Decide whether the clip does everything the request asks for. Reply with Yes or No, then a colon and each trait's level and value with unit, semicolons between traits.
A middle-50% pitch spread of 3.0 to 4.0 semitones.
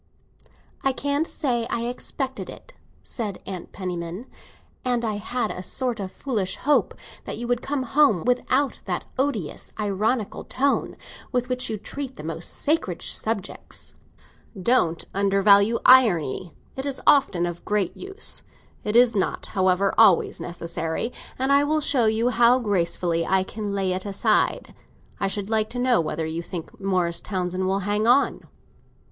No: average, 5.3 semitones